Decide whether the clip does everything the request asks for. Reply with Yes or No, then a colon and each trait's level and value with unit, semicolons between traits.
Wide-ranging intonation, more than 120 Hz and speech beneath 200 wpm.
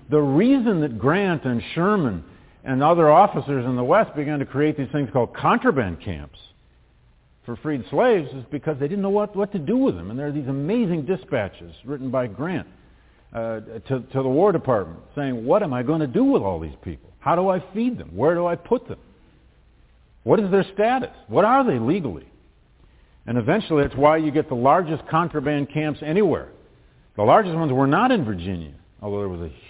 No: wide, 6.9 semitones; medium, 140 Hz; fast, 205 wpm